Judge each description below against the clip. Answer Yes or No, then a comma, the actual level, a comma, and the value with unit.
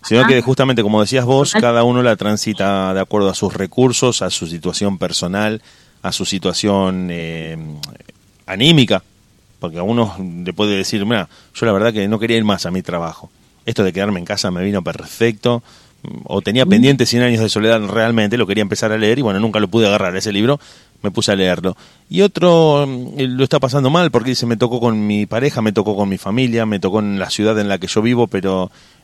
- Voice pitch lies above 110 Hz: No, low, 105 Hz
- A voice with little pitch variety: No, average, 3.7 semitones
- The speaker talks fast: Yes, fast, 215 wpm